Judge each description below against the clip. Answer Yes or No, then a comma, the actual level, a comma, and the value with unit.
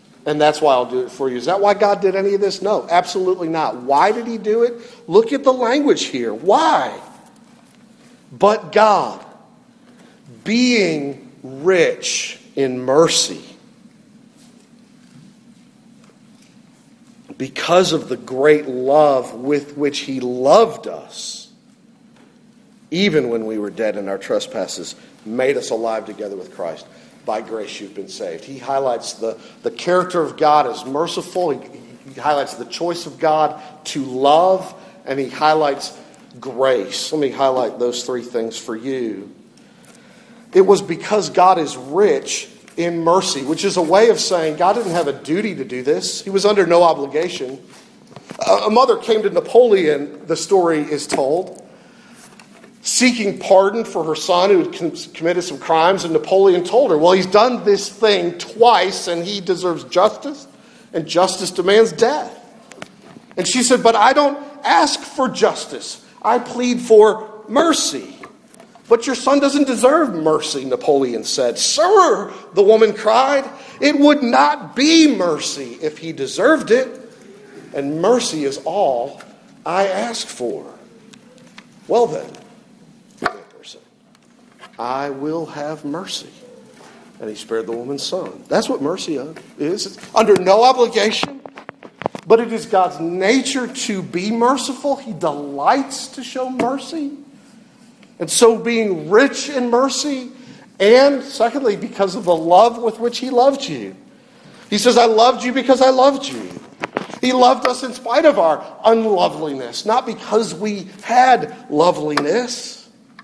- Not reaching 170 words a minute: Yes, average, 145 wpm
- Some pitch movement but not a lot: No, wide, 6.5 semitones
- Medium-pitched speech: No, high, 220 Hz